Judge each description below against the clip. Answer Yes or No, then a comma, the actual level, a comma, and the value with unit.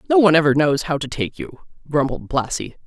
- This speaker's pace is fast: Yes, fast, 210 wpm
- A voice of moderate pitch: Yes, medium, 155 Hz